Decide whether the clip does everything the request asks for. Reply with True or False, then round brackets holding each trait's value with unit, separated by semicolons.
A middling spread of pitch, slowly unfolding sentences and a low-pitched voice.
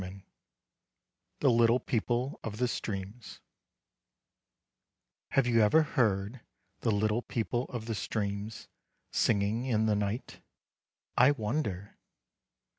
True (3.1 semitones; 110 wpm; 110 Hz)